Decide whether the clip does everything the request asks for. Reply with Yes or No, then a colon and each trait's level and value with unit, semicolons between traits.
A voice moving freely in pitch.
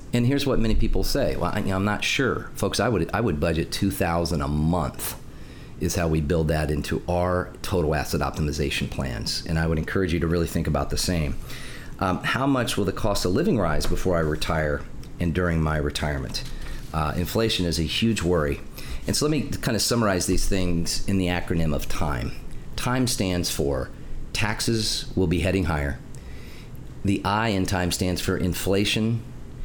No: average, 4.3 semitones